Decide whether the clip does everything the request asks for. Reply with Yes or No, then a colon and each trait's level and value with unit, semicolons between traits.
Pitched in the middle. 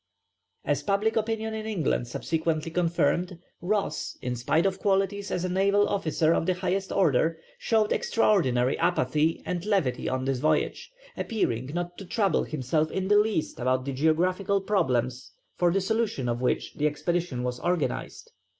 Yes: medium, 175 Hz